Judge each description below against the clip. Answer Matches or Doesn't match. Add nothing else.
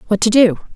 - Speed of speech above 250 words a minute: Doesn't match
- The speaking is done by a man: Doesn't match